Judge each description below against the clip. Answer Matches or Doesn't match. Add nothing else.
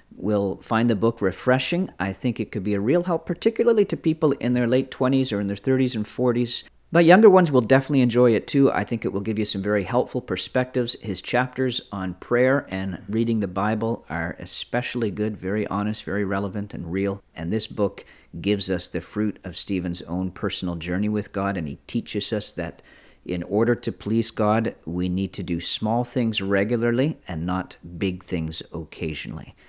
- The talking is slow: Doesn't match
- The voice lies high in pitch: Doesn't match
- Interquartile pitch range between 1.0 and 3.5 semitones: Doesn't match